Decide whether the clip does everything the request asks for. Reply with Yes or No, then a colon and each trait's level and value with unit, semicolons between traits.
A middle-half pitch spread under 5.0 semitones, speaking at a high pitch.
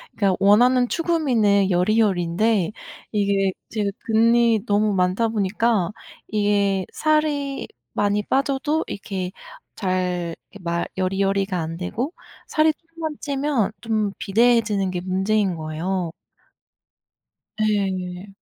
Yes: average, 3.9 semitones; high, 205 Hz